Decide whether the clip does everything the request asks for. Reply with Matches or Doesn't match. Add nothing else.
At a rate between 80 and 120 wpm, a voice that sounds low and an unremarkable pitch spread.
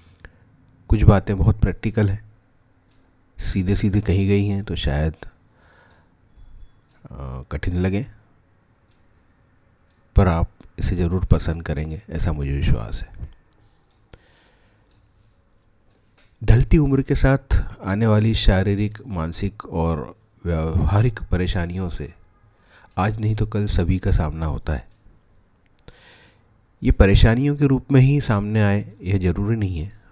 Matches